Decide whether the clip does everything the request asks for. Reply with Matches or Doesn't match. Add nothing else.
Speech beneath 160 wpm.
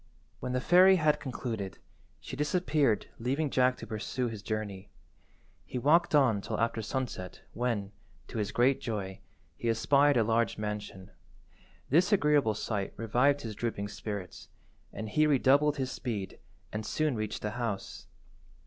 Matches